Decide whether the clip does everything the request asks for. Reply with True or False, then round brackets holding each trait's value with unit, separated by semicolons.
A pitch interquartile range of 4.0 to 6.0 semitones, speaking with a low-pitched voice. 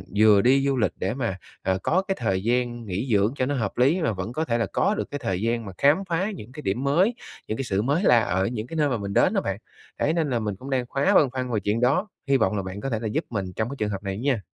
True (4.9 semitones; 120 Hz)